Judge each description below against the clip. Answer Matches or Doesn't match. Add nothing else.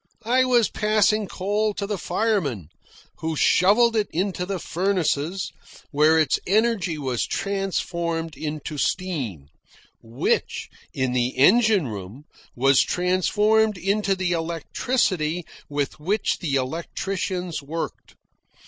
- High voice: Doesn't match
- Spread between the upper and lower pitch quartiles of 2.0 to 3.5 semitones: Doesn't match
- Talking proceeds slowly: Matches